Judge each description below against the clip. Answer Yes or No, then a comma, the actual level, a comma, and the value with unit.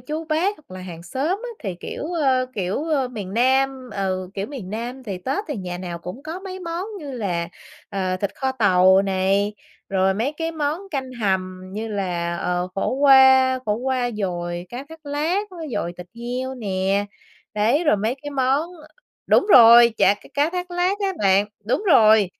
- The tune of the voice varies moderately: No, wide, 7.0 semitones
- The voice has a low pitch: No, high, 240 Hz